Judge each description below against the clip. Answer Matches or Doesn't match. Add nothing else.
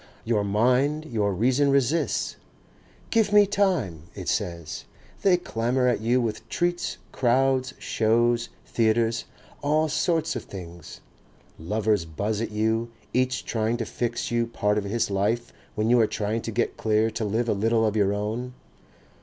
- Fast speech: Doesn't match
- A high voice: Doesn't match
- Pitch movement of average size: Matches